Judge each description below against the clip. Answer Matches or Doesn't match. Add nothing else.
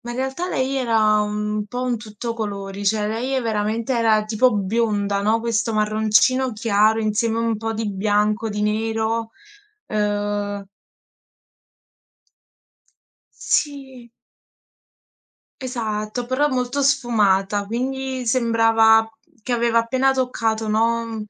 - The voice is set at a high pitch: Matches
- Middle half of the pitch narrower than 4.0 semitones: Matches